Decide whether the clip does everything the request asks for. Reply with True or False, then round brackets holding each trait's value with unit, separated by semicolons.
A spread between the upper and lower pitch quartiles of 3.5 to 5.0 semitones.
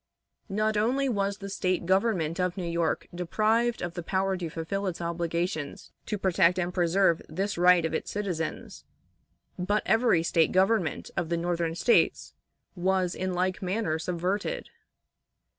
False (2.8 semitones)